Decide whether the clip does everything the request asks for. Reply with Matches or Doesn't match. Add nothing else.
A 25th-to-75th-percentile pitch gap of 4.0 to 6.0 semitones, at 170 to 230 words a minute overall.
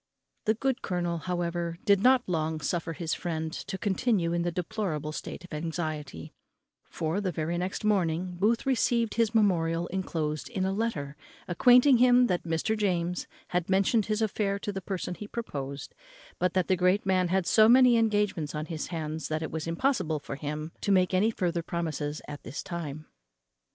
Matches